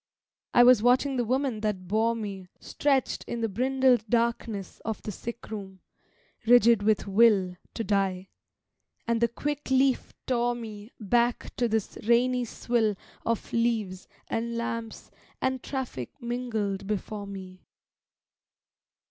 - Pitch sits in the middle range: No, high, 230 Hz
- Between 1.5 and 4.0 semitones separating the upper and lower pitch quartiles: Yes, average, 2.9 semitones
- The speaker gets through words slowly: Yes, slow, 130 wpm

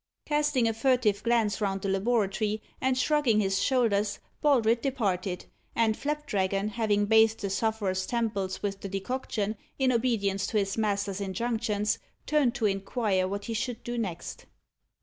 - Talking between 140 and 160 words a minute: Yes, average, 150 wpm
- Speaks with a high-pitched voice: Yes, high, 215 Hz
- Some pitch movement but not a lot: Yes, average, 3.3 semitones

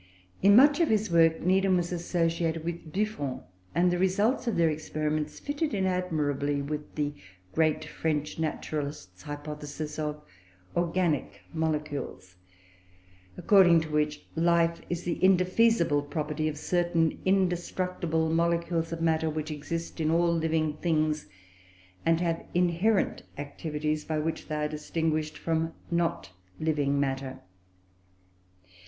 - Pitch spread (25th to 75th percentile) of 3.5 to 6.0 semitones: No, narrow, 2.5 semitones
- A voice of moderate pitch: Yes, medium, 160 Hz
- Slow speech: Yes, slow, 125 wpm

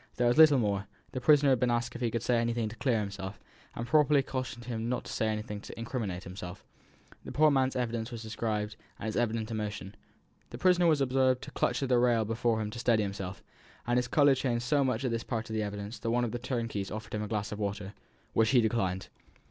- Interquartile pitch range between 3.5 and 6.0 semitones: No, average, 2.9 semitones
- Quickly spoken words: Yes, fast, 240 wpm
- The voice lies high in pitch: No, low, 115 Hz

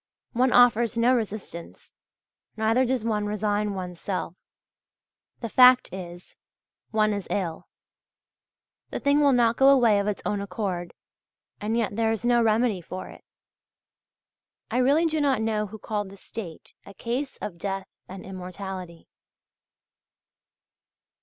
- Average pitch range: Yes, average, 3.9 semitones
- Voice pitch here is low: No, high, 215 Hz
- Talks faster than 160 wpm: No, average, 140 wpm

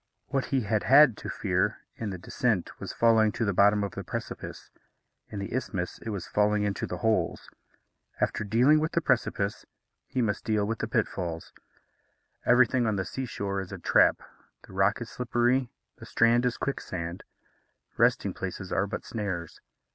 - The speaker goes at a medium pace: Yes, average, 175 wpm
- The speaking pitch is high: No, low, 105 Hz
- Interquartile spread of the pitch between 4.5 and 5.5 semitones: No, average, 3.5 semitones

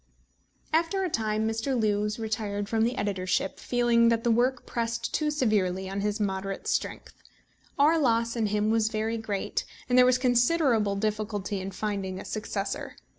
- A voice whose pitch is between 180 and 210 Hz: No, high, 220 Hz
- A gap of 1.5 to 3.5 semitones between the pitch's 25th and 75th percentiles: Yes, average, 2.9 semitones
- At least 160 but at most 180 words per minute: Yes, average, 165 wpm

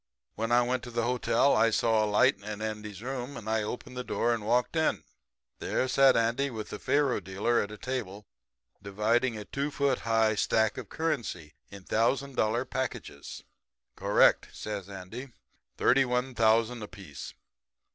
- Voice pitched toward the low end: Yes, low, 115 Hz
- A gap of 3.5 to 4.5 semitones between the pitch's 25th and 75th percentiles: No, average, 3.0 semitones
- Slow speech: No, average, 165 wpm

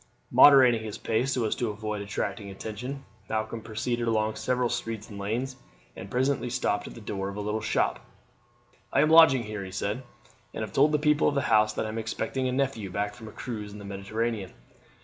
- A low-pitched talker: Yes, low, 110 Hz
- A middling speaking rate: No, fast, 210 wpm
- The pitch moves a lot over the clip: No, average, 3.4 semitones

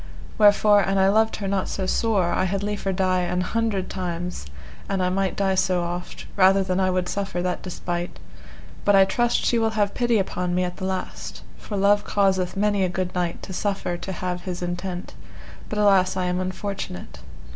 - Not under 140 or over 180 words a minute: No, average, 200 wpm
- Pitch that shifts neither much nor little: No, narrow, 1.9 semitones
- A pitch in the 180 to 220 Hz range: Yes, high, 190 Hz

